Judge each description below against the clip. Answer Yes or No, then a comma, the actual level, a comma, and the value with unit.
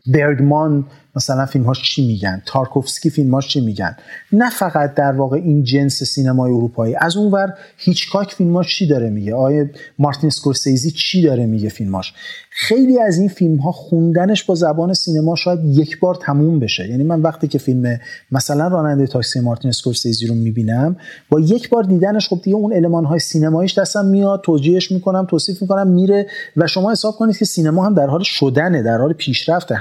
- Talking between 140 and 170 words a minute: No, average, 180 wpm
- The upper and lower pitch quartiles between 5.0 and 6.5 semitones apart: Yes, wide, 5.5 semitones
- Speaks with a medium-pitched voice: Yes, medium, 155 Hz